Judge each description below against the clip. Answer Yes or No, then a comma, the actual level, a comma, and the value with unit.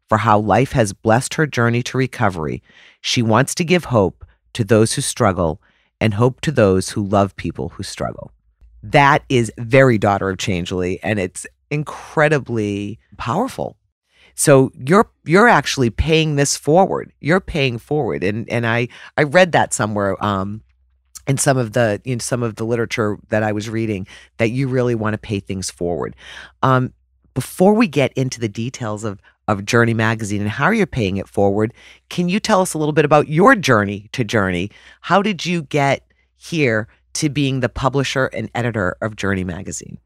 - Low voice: Yes, low, 115 Hz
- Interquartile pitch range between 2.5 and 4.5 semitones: No, average, 5.2 semitones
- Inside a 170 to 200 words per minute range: Yes, average, 180 wpm